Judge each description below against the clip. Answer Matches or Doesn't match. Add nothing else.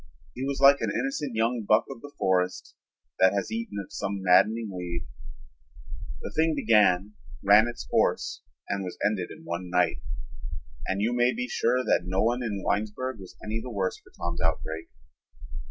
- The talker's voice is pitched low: Matches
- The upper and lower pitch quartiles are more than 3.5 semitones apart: Matches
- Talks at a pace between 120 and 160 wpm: Doesn't match